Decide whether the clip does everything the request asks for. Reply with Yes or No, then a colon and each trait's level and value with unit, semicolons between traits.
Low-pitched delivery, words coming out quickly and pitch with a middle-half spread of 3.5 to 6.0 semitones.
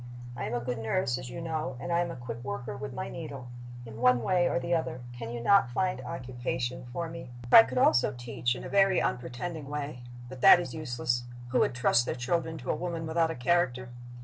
Yes: low, 130 Hz; fast, 230 wpm; average, 5.2 semitones